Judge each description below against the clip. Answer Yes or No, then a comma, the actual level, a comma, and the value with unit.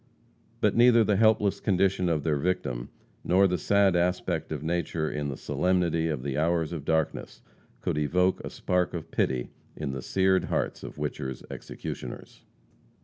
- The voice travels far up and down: No, average, 3.8 semitones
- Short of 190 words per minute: Yes, average, 160 wpm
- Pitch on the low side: Yes, very low, 85 Hz